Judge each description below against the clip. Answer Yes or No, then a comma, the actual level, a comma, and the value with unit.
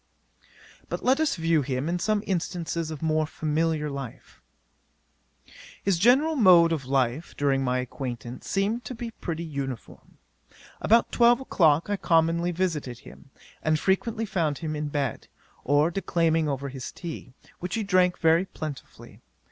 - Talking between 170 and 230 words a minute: No, average, 150 wpm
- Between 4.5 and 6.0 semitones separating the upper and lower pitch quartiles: Yes, average, 4.8 semitones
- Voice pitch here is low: No, medium, 165 Hz